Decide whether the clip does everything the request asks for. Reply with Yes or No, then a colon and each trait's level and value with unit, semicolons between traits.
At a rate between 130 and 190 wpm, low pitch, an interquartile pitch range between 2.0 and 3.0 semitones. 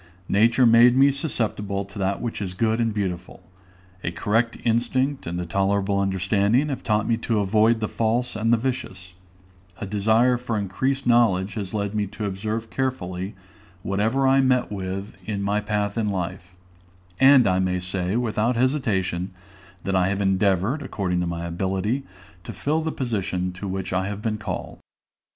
No: average, 170 wpm; low, 105 Hz; average, 3.8 semitones